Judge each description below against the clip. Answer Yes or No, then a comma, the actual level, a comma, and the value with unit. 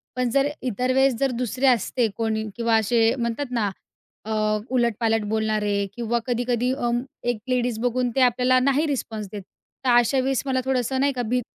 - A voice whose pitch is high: Yes, high, 245 Hz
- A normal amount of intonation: No, narrow, 2.3 semitones